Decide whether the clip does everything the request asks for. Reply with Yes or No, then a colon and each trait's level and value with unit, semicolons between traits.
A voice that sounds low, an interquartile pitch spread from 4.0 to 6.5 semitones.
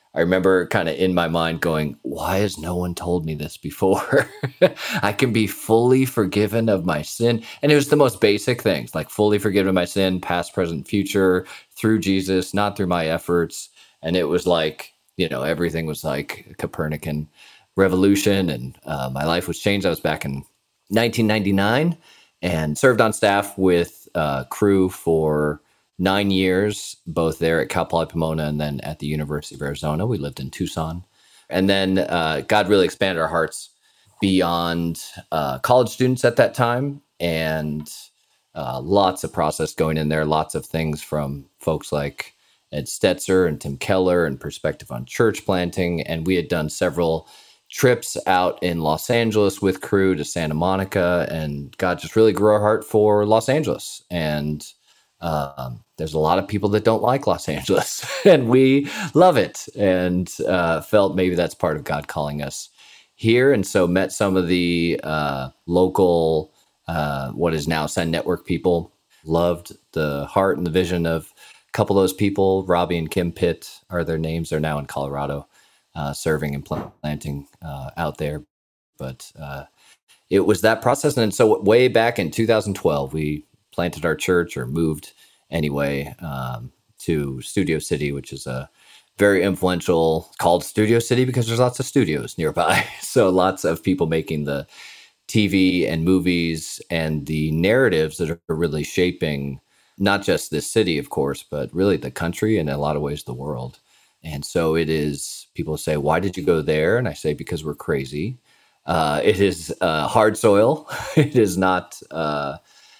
Yes: very low, 85 Hz; average, 4.6 semitones